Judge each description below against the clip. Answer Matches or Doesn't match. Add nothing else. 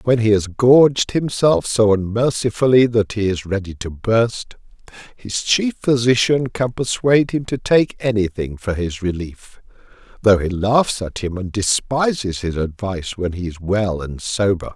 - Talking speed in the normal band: Matches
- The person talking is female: Doesn't match